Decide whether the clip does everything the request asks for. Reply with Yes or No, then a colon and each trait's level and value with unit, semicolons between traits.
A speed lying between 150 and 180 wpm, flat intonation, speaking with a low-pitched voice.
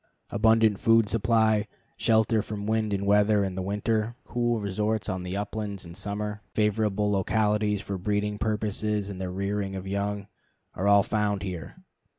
Yes: average, 155 wpm; narrow, 1.4 semitones; low, 105 Hz